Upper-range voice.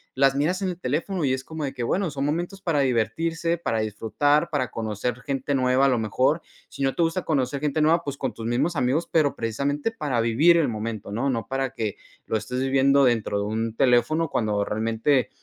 No: low, 135 Hz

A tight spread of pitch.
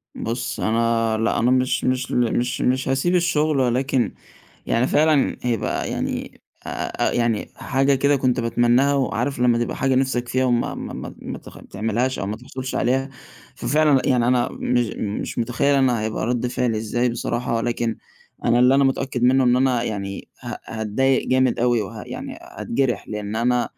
Yes: narrow, 2.2 semitones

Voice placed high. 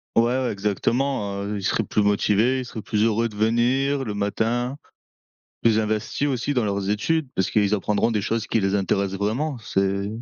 No: low, 110 Hz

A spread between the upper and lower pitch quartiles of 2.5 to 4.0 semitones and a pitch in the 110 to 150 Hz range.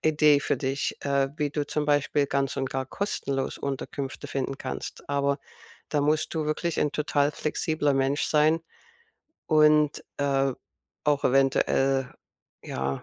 No: narrow, 1.9 semitones; medium, 140 Hz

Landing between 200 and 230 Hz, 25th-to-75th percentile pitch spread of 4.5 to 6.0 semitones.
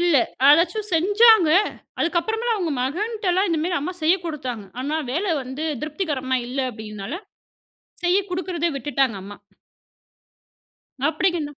No: very high, 330 Hz; average, 5.2 semitones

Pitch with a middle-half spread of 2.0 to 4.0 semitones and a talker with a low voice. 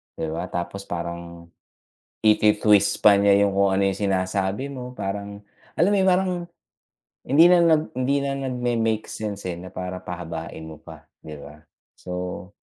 No: average, 4.9 semitones; low, 100 Hz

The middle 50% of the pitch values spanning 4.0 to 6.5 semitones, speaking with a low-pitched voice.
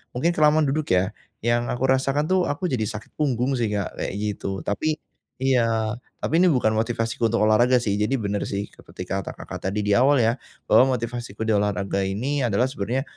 Yes: average, 4.4 semitones; low, 120 Hz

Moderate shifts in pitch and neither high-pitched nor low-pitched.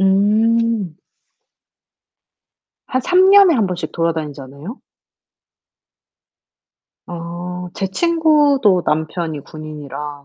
No: wide, 6.7 semitones; medium, 180 Hz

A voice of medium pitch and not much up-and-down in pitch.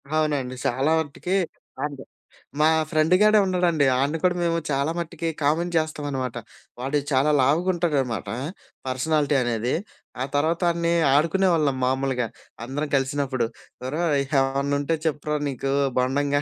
No: medium, 145 Hz; average, 3.5 semitones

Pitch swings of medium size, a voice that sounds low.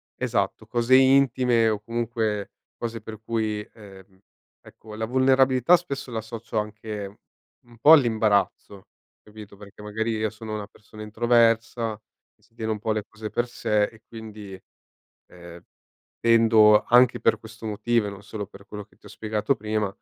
No: narrow, 1.8 semitones; low, 110 Hz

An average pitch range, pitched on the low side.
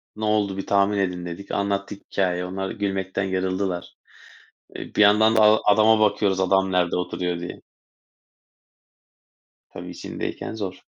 No: narrow, 1.8 semitones; very low, 95 Hz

